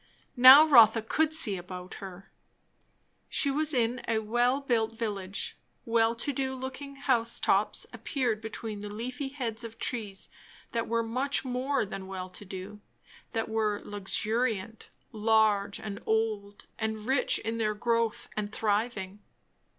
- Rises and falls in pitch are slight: No, average, 3.1 semitones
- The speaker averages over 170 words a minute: No, average, 145 wpm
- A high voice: Yes, high, 225 Hz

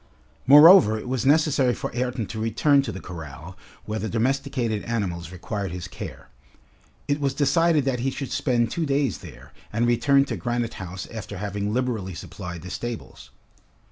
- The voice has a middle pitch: No, low, 120 Hz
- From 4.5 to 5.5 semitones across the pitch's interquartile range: Yes, average, 5.2 semitones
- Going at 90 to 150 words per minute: No, average, 170 wpm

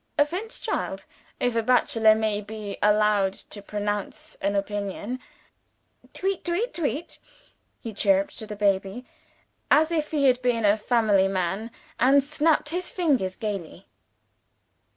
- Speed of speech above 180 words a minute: No, slow, 135 wpm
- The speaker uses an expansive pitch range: Yes, wide, 5.8 semitones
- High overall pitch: Yes, high, 220 Hz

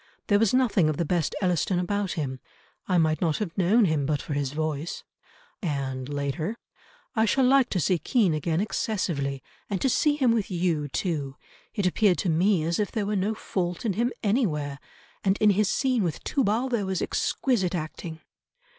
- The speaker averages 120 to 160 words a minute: No, average, 190 wpm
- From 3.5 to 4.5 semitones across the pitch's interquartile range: No, wide, 5.4 semitones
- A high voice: No, medium, 180 Hz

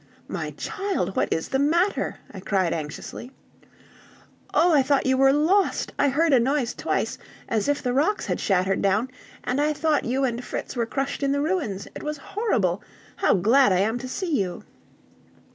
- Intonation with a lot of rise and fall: Yes, wide, 5.9 semitones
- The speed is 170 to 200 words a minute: Yes, average, 185 wpm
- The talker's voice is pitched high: Yes, very high, 265 Hz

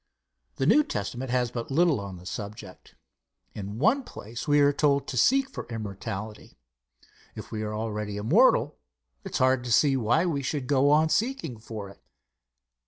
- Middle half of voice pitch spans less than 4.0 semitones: No, wide, 5.4 semitones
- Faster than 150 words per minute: Yes, average, 170 wpm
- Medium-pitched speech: No, low, 125 Hz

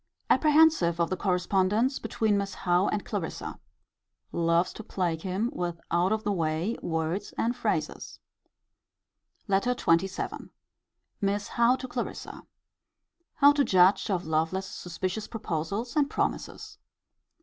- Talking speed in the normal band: No, slow, 125 wpm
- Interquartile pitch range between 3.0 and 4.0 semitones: No, average, 4.5 semitones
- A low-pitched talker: No, high, 195 Hz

